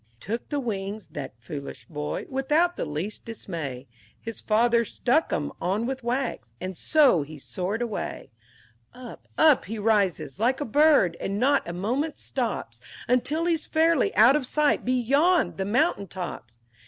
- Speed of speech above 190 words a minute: No, average, 165 wpm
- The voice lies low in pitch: No, high, 230 Hz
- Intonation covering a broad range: Yes, wide, 7.2 semitones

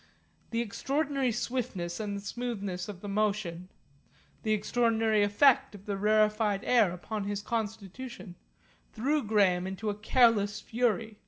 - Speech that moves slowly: Yes, slow, 130 wpm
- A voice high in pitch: Yes, high, 215 Hz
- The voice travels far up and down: No, average, 2.7 semitones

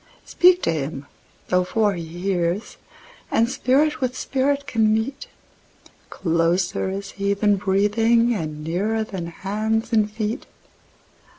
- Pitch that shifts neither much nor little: Yes, average, 4.1 semitones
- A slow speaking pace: Yes, slow, 120 wpm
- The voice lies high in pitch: Yes, high, 205 Hz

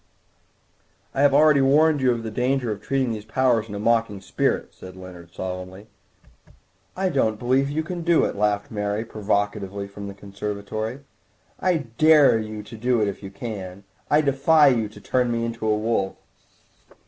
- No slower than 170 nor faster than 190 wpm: Yes, average, 175 wpm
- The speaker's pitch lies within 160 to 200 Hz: No, low, 110 Hz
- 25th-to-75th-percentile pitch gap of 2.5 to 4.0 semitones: No, average, 4.8 semitones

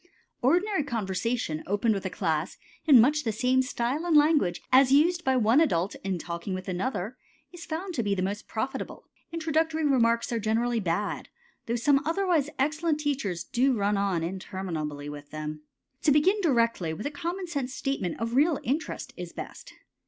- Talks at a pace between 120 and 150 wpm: No, average, 175 wpm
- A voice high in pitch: Yes, high, 240 Hz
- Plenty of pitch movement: Yes, wide, 7.6 semitones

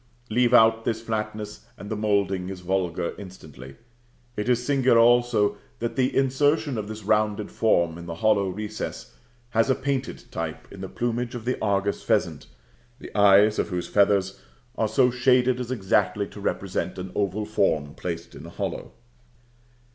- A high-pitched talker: No, low, 105 Hz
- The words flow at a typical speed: Yes, average, 165 wpm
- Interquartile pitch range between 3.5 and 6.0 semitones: Yes, average, 3.8 semitones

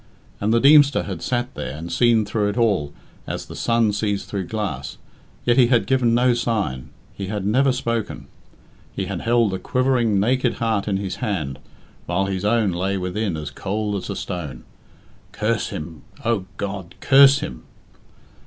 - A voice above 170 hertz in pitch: No, low, 105 Hz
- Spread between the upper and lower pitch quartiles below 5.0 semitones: Yes, average, 4.0 semitones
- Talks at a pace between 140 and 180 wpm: Yes, average, 170 wpm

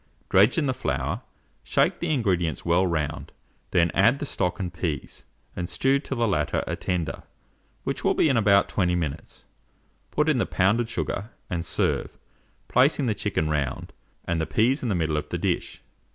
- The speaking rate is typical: Yes, average, 180 wpm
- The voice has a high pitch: No, very low, 95 Hz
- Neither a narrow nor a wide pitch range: No, wide, 6.1 semitones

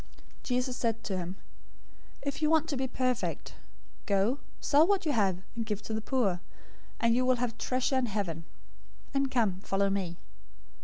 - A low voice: No, high, 230 Hz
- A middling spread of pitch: Yes, average, 4.9 semitones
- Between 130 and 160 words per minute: No, average, 175 wpm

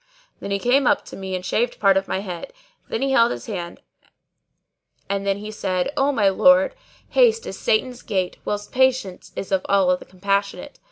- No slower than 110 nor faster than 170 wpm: No, average, 190 wpm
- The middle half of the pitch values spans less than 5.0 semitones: No, average, 5.3 semitones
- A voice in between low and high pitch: No, high, 200 Hz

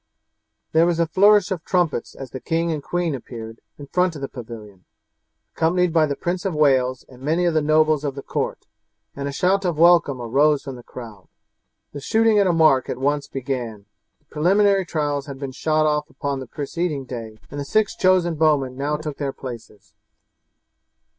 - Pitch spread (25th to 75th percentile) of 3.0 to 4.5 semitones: Yes, average, 4.2 semitones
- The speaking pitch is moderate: Yes, medium, 150 Hz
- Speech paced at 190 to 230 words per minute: Yes, average, 195 wpm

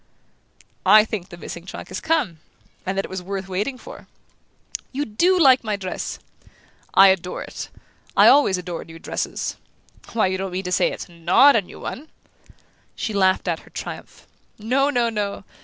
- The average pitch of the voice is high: Yes, high, 195 Hz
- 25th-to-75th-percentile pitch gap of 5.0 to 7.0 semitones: Yes, average, 5.3 semitones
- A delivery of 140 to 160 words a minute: No, average, 175 wpm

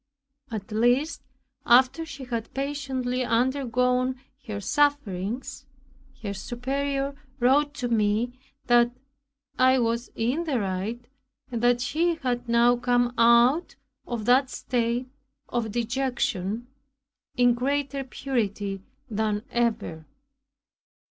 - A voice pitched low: No, high, 245 Hz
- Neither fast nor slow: No, slow, 105 wpm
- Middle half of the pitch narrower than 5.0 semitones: Yes, narrow, 2.5 semitones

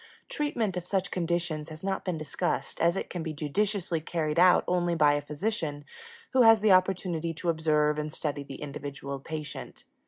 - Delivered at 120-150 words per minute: No, average, 180 wpm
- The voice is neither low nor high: Yes, medium, 165 Hz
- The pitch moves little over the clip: No, average, 3.5 semitones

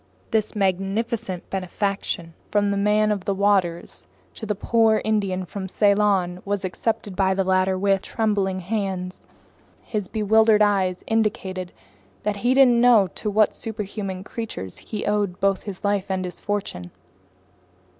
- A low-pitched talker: No, high, 200 Hz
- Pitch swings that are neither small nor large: No, narrow, 2.1 semitones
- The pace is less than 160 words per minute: Yes, average, 145 wpm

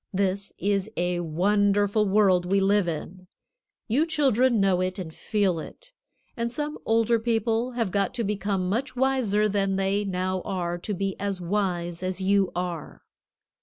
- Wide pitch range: No, average, 3.1 semitones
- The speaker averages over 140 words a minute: Yes, average, 160 wpm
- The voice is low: No, high, 200 Hz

